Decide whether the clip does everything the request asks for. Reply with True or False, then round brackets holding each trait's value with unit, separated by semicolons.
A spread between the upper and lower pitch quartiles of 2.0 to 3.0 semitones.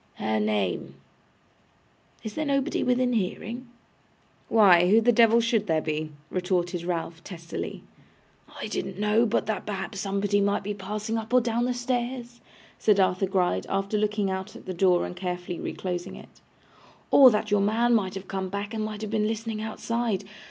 False (3.6 semitones)